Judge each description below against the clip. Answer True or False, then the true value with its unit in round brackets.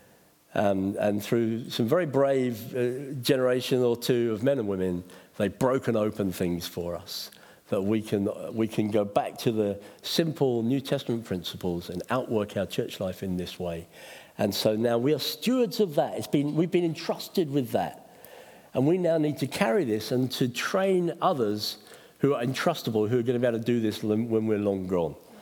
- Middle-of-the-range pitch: False (120 Hz)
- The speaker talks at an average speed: True (195 wpm)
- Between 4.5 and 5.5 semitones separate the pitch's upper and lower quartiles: True (5.2 semitones)